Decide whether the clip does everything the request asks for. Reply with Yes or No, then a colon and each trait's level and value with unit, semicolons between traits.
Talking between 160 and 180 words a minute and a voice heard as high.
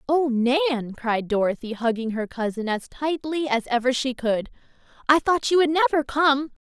Yes: average, 170 wpm; very high, 260 Hz